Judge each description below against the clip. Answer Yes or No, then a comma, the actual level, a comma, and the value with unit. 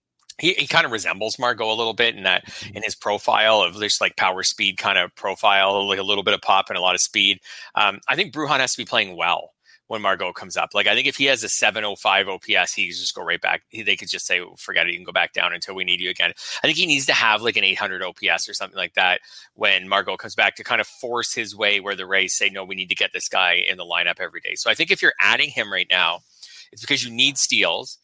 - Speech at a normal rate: No, fast, 280 wpm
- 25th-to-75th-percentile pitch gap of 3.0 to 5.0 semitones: Yes, average, 3.7 semitones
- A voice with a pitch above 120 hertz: No, low, 100 Hz